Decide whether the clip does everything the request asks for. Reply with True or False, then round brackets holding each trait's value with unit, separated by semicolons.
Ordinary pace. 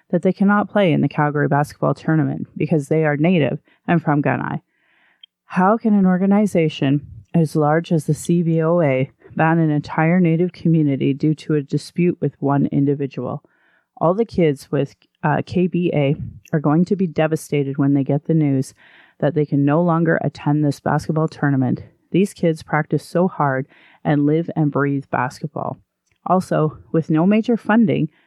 True (165 wpm)